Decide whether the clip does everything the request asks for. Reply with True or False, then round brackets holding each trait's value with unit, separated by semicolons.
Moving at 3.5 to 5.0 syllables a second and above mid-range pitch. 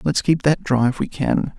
False (4.7 syllables/s; 145 Hz)